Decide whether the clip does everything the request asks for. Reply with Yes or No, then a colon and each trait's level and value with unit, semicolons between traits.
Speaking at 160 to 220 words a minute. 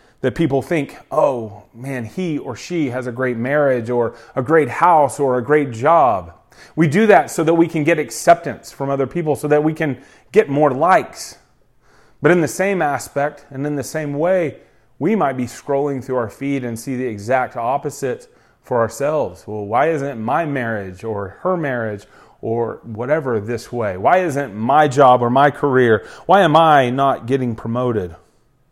Yes: average, 185 wpm